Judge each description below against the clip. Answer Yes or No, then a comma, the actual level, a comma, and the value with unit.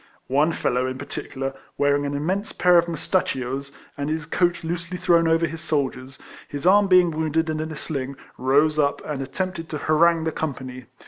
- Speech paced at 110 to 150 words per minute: No, average, 185 wpm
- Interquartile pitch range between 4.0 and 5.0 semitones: No, average, 3.3 semitones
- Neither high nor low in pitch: Yes, medium, 155 Hz